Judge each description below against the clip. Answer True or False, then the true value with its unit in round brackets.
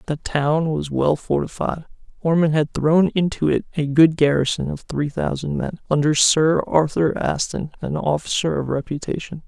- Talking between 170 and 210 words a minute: False (160 wpm)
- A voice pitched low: False (155 Hz)